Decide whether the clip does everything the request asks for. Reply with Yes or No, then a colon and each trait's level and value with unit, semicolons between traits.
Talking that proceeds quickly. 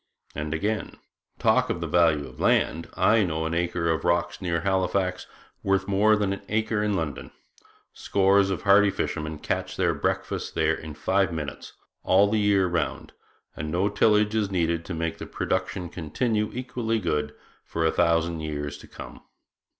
No: average, 170 wpm